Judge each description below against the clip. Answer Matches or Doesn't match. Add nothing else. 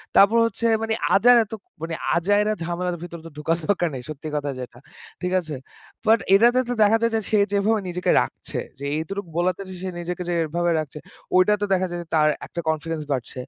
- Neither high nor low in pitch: Matches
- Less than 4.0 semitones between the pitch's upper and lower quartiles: Doesn't match